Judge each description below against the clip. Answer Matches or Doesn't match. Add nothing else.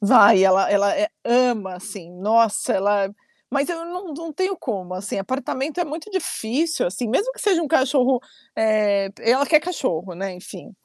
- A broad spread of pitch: Matches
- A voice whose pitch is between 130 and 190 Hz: Doesn't match